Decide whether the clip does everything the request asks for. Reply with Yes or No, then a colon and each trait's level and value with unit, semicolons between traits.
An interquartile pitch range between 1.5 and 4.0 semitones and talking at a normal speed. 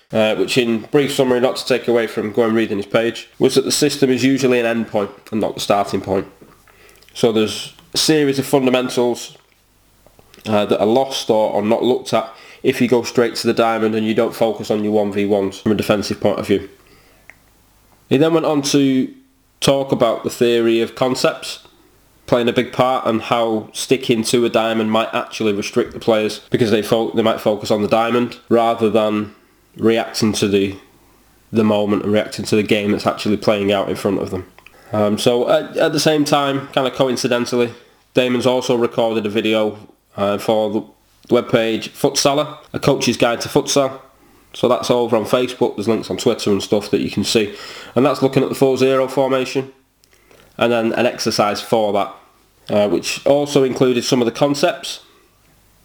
Yes: average, 3.4 semitones; average, 195 wpm